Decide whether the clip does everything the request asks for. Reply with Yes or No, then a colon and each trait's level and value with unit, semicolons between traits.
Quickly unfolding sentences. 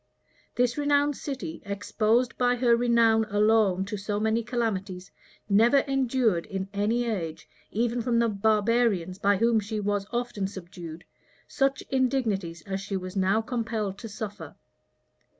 No: average, 140 wpm